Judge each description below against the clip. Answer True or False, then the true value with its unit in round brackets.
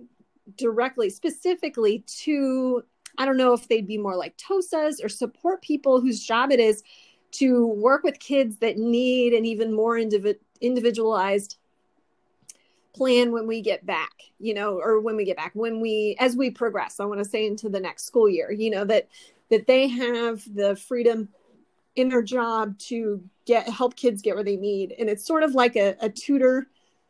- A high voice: True (230 Hz)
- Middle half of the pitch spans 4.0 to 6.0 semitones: False (3.2 semitones)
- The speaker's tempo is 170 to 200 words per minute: True (185 wpm)